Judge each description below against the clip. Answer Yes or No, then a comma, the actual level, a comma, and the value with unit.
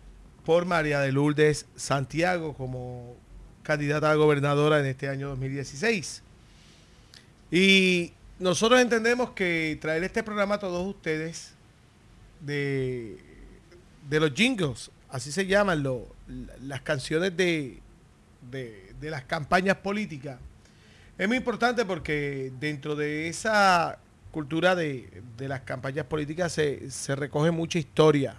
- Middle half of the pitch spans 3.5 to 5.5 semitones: Yes, average, 4.7 semitones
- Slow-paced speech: Yes, slow, 120 wpm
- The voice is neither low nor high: Yes, medium, 150 Hz